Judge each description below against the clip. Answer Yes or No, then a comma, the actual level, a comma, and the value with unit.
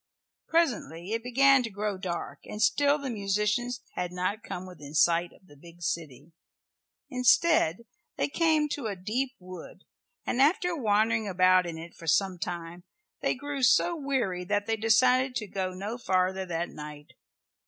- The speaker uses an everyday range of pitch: No, wide, 5.9 semitones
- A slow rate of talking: No, average, 165 wpm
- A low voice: No, high, 205 Hz